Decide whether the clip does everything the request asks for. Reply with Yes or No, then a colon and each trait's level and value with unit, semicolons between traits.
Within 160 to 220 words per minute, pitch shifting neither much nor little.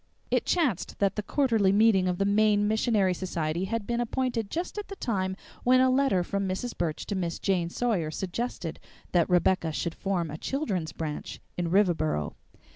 Yes: average, 180 wpm; average, 4.8 semitones